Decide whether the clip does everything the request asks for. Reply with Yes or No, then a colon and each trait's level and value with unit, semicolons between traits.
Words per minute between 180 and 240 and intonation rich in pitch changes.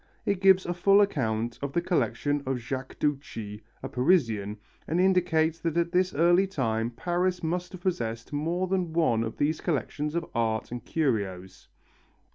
No: average, 165 wpm; wide, 7.2 semitones